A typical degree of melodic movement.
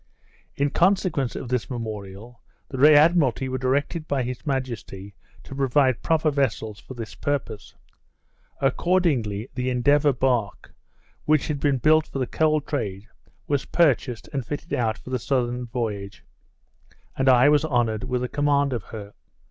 Yes: average, 3.6 semitones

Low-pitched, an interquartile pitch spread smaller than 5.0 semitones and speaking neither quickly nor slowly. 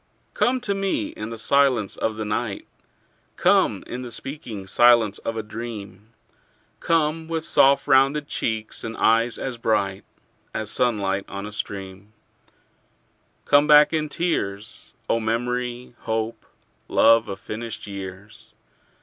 No: low, 115 Hz; average, 4.2 semitones; slow, 130 wpm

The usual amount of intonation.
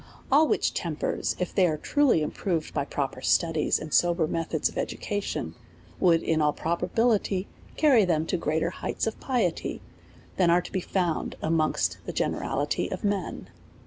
Yes: average, 4.2 semitones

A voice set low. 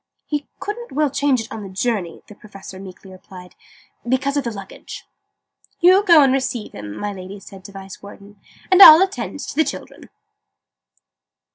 No: high, 215 Hz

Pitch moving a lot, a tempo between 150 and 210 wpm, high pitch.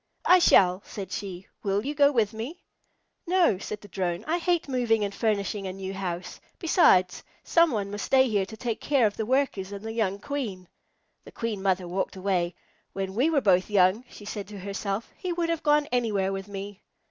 No: average, 5.0 semitones; average, 200 wpm; high, 205 Hz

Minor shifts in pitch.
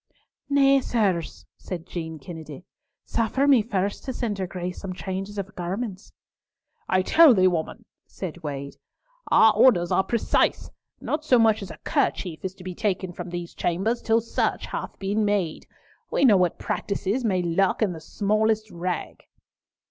No: average, 3.9 semitones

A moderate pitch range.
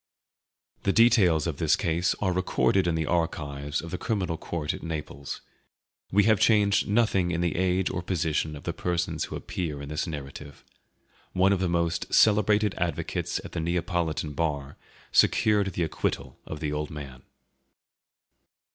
Yes: average, 3.6 semitones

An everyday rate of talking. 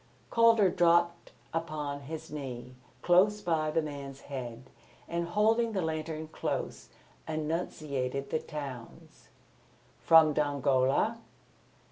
No: slow, 100 wpm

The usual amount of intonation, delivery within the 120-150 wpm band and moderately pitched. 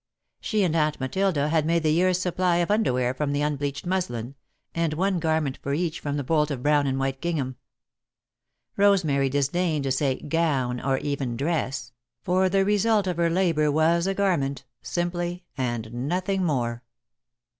No: average, 4.5 semitones; average, 165 wpm; medium, 155 Hz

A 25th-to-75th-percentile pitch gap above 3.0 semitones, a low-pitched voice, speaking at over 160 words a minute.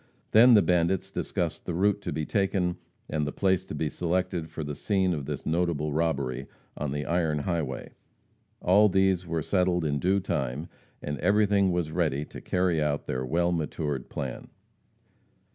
Yes: average, 3.8 semitones; very low, 85 Hz; average, 170 wpm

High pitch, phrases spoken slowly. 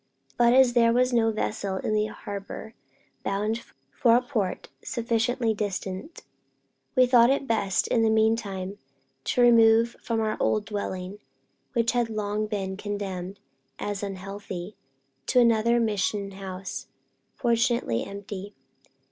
Yes: high, 215 Hz; slow, 130 wpm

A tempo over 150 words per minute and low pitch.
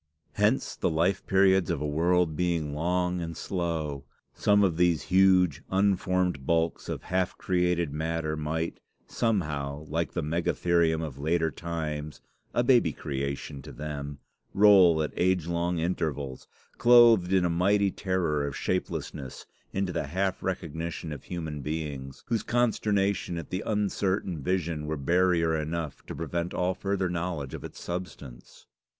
No: average, 145 wpm; very low, 85 Hz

